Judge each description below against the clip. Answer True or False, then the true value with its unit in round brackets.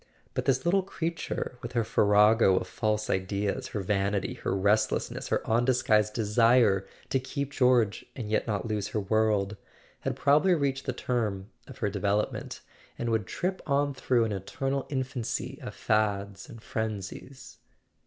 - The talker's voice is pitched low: True (110 Hz)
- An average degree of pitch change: True (4.1 semitones)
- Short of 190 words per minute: True (155 wpm)